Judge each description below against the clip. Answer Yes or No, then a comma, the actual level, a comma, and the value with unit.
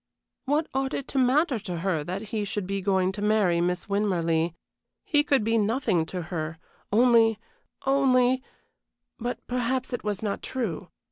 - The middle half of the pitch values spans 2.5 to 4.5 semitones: No, wide, 5.4 semitones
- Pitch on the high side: Yes, high, 215 Hz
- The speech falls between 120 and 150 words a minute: No, average, 160 wpm